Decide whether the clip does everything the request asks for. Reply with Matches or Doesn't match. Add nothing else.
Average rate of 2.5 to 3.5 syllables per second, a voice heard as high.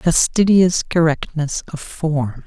Doesn't match